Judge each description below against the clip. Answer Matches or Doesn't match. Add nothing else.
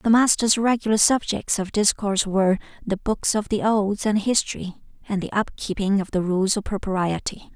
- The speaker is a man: Doesn't match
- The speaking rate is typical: Matches